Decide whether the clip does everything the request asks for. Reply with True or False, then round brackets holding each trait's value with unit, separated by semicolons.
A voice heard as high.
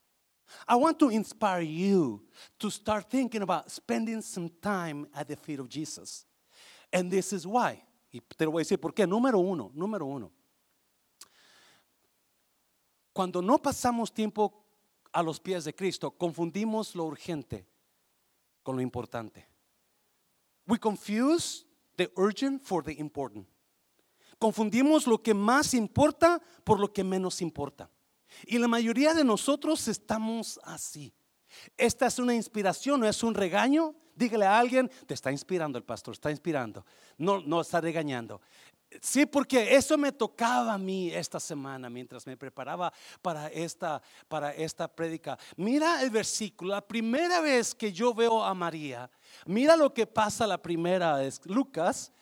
True (200 Hz)